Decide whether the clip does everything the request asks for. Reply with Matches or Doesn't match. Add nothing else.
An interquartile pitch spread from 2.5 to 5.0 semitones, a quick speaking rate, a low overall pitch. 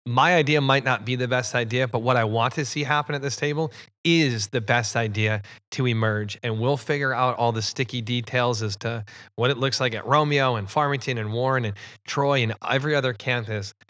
Matches